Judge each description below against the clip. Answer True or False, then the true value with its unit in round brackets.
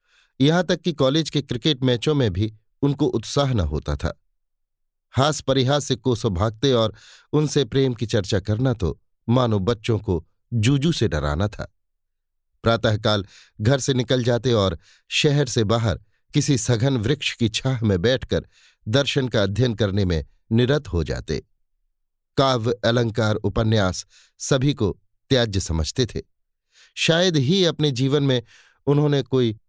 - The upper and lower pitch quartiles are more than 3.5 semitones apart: True (5.5 semitones)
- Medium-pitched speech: False (115 Hz)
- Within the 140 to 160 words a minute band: True (145 wpm)